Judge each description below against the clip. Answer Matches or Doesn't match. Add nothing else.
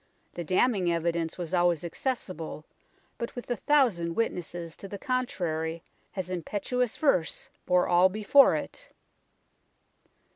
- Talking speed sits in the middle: Doesn't match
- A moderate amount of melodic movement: Doesn't match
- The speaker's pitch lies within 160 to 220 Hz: Matches